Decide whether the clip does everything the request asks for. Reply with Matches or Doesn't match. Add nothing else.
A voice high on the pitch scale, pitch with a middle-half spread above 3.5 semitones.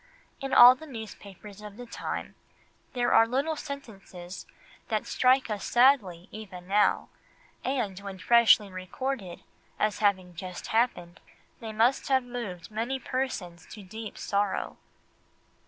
Matches